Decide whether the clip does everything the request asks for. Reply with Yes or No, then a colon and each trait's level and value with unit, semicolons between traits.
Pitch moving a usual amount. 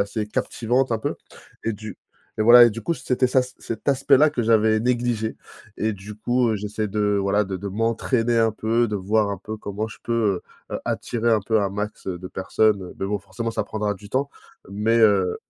No: narrow, 2.2 semitones